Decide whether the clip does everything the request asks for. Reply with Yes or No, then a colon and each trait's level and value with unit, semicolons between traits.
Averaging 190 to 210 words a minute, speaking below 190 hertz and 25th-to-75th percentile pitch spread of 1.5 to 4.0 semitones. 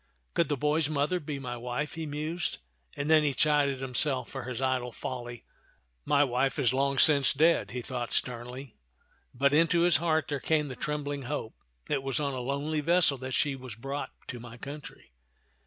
Yes: average, 195 wpm; medium, 140 Hz; average, 3.0 semitones